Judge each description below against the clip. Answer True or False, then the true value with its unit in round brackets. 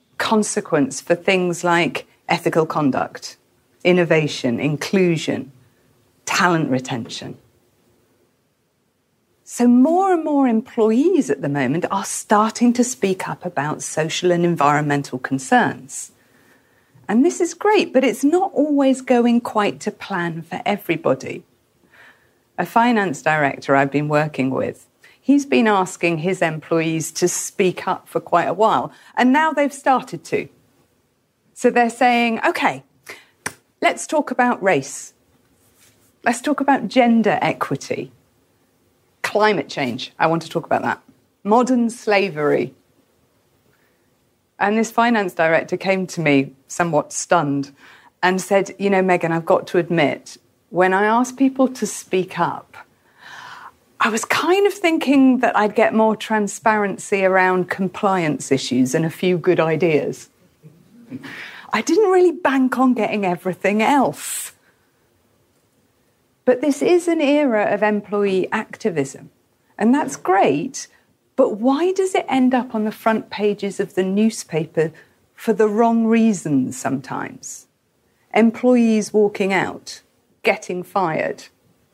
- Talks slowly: True (125 wpm)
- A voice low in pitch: False (195 Hz)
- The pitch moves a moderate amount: False (7.2 semitones)